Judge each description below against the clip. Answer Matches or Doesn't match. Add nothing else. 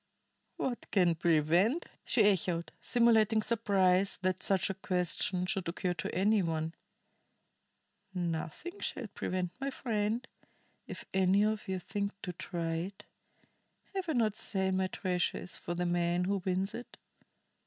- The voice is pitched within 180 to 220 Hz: Matches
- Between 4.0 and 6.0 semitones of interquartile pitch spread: Doesn't match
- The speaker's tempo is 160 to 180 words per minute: Doesn't match